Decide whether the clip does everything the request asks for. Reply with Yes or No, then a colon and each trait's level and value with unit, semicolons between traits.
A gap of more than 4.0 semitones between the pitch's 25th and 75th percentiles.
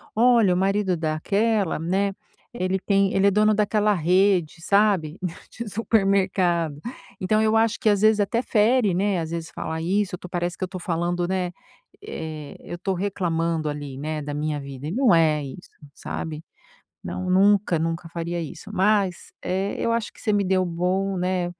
No: average, 3.6 semitones